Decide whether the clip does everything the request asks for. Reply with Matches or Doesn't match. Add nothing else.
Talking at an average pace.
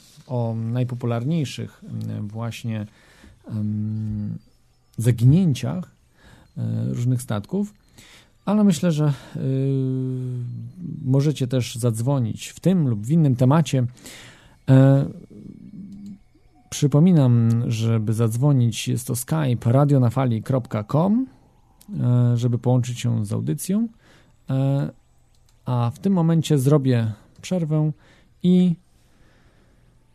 Doesn't match